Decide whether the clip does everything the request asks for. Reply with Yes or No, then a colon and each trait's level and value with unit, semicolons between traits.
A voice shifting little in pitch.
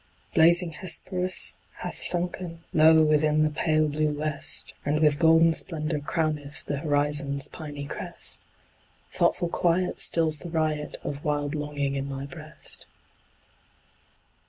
Yes: narrow, 2.0 semitones